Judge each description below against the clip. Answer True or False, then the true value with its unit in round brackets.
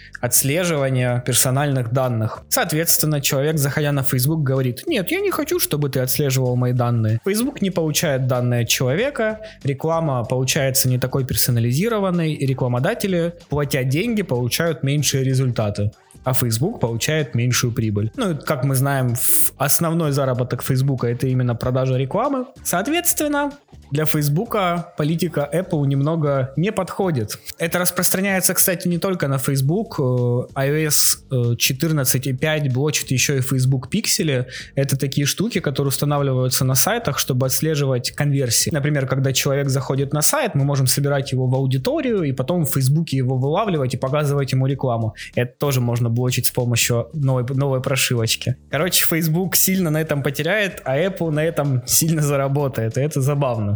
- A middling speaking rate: True (145 wpm)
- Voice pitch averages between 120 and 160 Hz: True (140 Hz)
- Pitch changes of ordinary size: True (3.9 semitones)